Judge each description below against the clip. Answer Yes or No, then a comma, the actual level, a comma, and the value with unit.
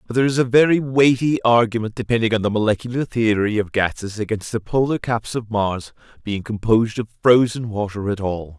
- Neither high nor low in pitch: No, low, 110 Hz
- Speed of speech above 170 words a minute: Yes, average, 190 wpm